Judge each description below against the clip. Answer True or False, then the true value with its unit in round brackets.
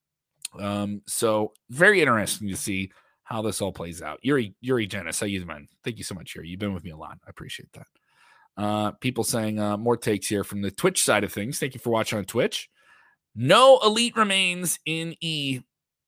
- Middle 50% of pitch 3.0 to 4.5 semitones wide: False (5.4 semitones)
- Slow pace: False (205 wpm)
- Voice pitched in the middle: False (105 Hz)